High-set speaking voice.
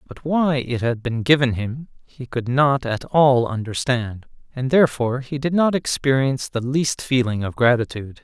No: low, 130 Hz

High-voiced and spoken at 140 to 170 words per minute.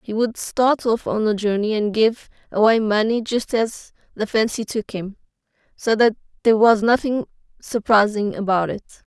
Yes: high, 220 Hz; average, 165 wpm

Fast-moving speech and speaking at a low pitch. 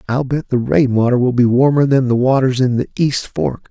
Yes: fast, 225 wpm; low, 125 Hz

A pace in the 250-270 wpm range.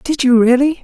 No: fast, 215 wpm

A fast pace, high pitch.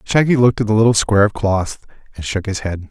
No: fast, 250 wpm; low, 105 Hz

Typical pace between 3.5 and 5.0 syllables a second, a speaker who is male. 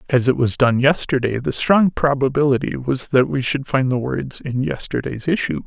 Yes: 4.9 syllables/s; male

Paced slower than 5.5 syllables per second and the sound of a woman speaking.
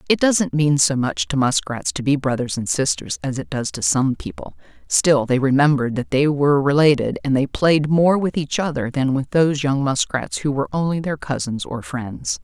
Yes: 5.1 syllables/s; female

